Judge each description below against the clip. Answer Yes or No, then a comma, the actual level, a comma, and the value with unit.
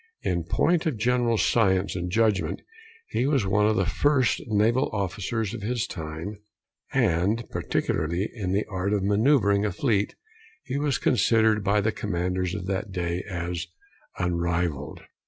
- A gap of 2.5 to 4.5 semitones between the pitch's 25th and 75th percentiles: Yes, average, 3.9 semitones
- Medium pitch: No, low, 100 Hz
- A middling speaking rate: Yes, average, 150 wpm